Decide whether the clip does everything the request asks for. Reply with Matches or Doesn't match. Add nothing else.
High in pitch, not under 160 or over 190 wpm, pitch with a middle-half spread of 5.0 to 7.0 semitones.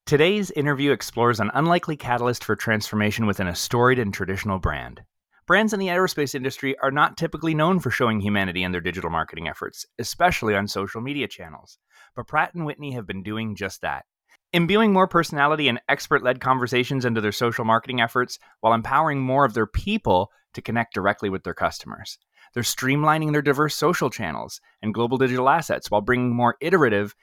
Doesn't match